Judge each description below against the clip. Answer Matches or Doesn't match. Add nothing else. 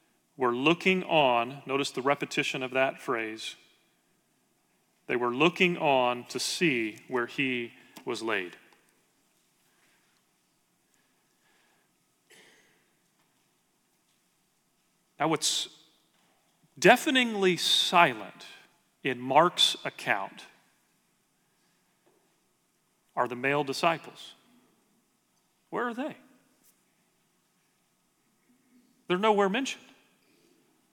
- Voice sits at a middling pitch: Matches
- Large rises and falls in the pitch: Matches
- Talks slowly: Matches